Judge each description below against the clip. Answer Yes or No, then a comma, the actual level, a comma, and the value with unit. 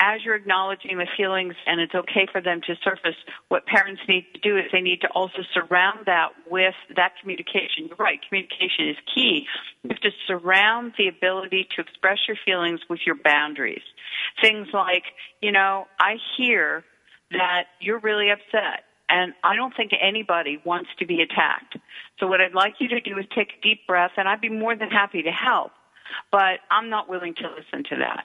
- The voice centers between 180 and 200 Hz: Yes, high, 190 Hz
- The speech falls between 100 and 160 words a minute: No, average, 195 wpm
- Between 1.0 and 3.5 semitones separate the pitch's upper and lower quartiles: Yes, average, 3.0 semitones